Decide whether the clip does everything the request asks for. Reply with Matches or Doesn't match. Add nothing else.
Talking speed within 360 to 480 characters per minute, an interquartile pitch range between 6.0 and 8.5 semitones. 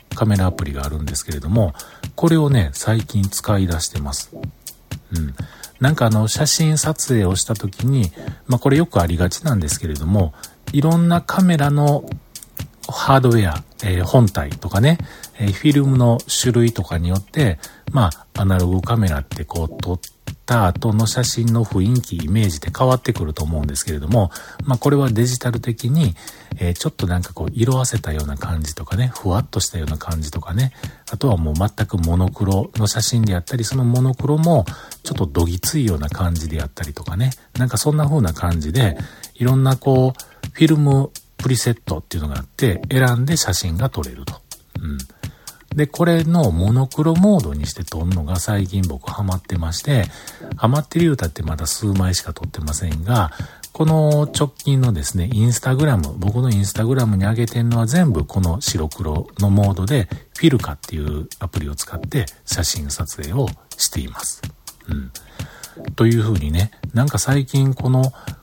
Matches